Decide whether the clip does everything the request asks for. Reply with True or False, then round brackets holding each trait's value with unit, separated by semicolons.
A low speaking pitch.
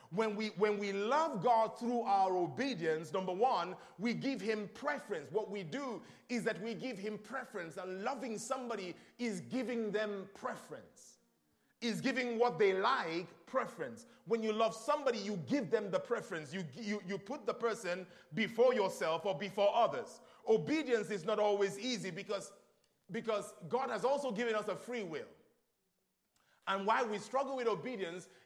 False (220 Hz)